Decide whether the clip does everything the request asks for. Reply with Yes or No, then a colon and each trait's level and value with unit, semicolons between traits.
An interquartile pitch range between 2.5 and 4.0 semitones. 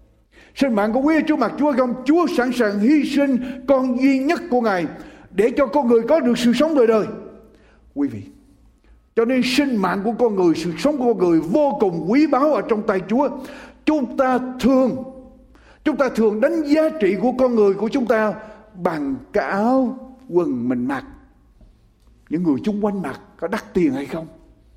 No: average, 4.5 semitones